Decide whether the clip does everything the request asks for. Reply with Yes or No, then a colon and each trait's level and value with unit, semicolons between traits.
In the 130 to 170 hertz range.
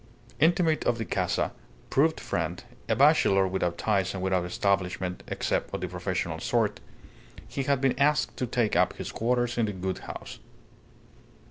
No: low, 100 Hz